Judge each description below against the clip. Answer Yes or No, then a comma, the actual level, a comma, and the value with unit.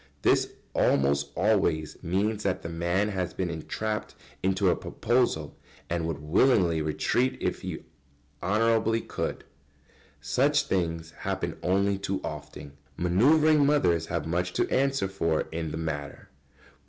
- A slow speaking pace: Yes, slow, 130 wpm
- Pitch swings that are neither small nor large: Yes, average, 4.9 semitones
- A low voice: Yes, very low, 90 Hz